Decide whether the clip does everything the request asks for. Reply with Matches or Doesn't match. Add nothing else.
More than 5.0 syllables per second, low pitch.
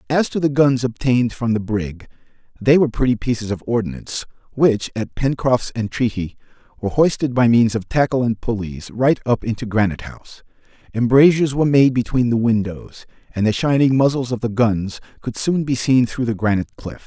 Matches